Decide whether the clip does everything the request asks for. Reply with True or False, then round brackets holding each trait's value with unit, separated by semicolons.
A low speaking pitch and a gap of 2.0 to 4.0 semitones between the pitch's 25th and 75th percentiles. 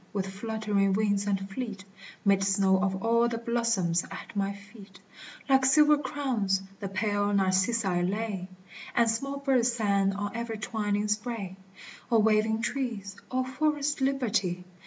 False (210 Hz; 3.3 semitones)